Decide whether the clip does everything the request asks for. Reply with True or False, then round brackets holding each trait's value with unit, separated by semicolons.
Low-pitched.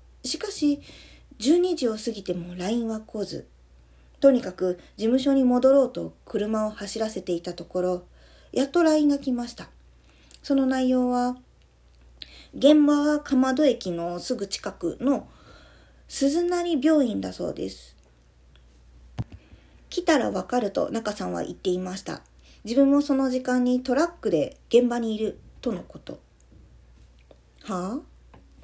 False (230 Hz)